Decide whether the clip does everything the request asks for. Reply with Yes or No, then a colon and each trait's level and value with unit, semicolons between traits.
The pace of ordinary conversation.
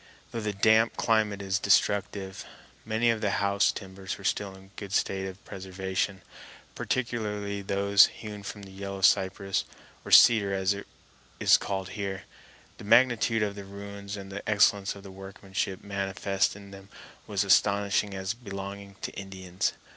Yes: average, 160 wpm